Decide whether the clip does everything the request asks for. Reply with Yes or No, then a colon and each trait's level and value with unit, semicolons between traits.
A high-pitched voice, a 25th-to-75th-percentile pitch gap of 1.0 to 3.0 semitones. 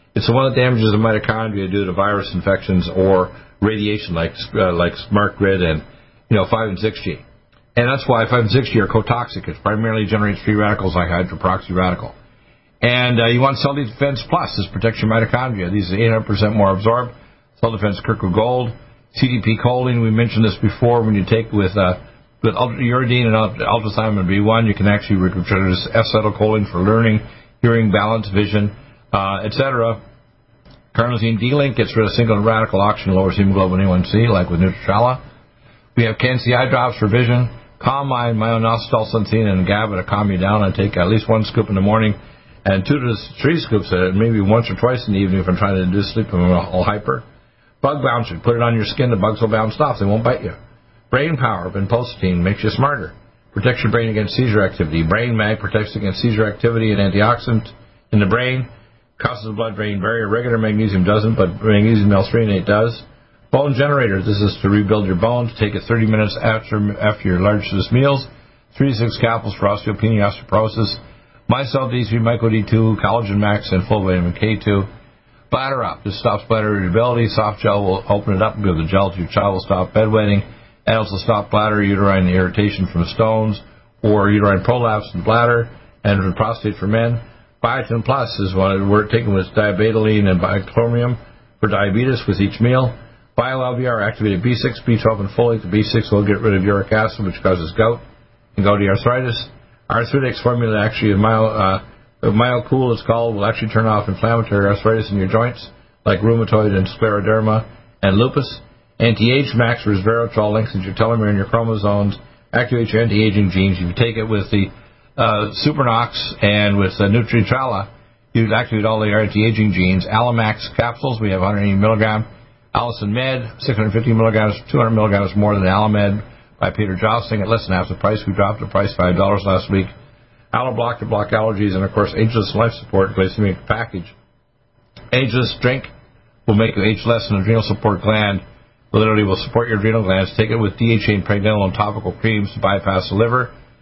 No: low, 110 Hz; average, 2.7 semitones